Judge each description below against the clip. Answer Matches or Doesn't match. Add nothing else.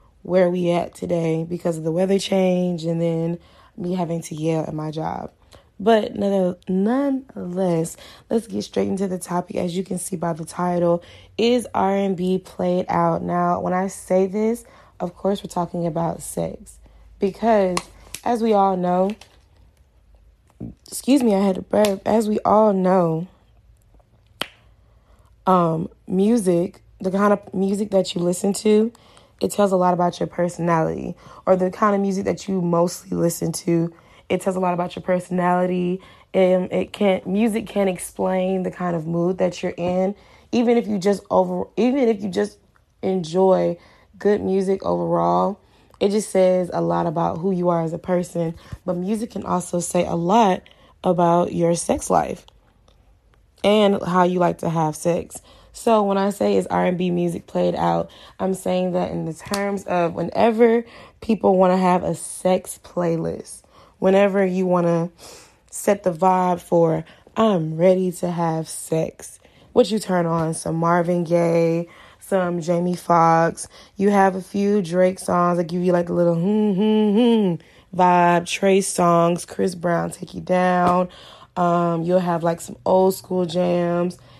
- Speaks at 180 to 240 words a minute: Doesn't match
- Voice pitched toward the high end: Doesn't match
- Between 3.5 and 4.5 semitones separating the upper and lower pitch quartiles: Doesn't match